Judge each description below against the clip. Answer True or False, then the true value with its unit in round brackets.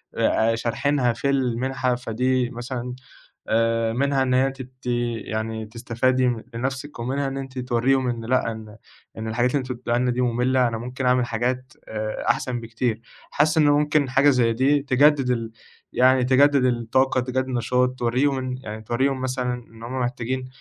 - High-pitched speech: False (125 Hz)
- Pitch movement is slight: True (2.0 semitones)